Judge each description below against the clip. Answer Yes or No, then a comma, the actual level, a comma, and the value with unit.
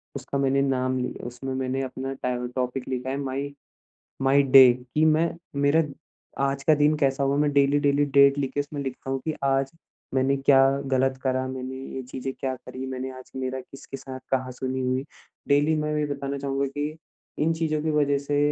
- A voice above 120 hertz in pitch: Yes, low, 135 Hz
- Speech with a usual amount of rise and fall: No, narrow, 1.5 semitones